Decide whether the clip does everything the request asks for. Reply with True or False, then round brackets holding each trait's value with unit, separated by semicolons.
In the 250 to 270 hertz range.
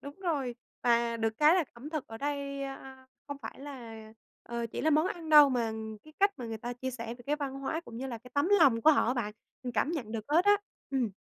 True (265 Hz)